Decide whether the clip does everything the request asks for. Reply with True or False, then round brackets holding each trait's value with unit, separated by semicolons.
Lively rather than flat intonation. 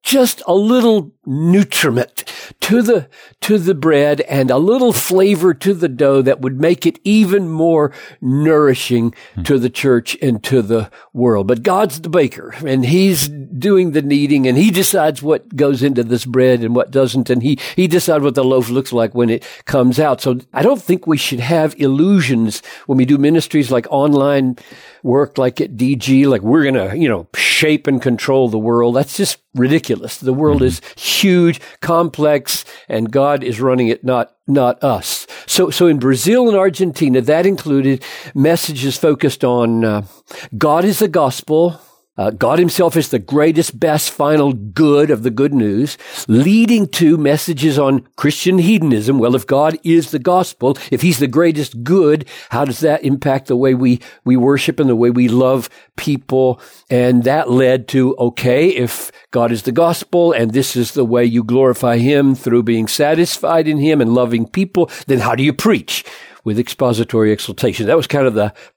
False (4.5 semitones)